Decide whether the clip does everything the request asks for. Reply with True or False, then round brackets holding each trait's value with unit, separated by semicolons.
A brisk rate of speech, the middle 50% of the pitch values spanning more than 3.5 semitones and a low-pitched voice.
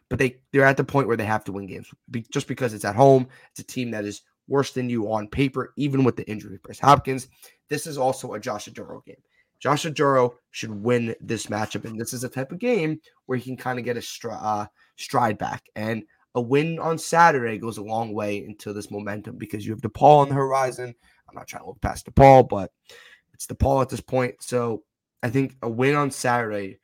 True (235 wpm; 3.9 semitones; 125 Hz)